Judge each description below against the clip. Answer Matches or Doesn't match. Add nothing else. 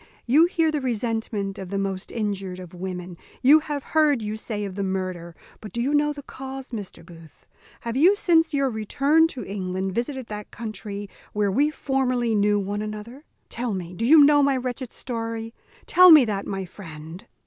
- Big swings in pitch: Matches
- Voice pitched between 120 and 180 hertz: Doesn't match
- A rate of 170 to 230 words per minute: Matches